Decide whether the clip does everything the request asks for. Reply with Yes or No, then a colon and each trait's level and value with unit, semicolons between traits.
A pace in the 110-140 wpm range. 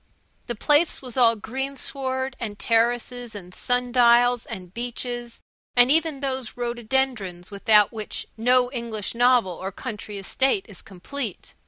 Yes: slow, 135 wpm